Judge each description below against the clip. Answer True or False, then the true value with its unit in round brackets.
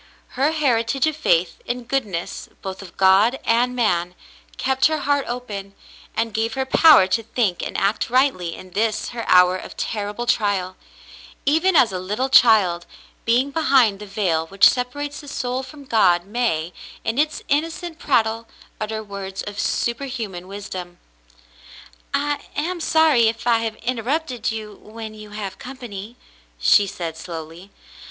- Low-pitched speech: False (225 Hz)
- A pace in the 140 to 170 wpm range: True (155 wpm)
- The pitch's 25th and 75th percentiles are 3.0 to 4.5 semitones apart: False (5.2 semitones)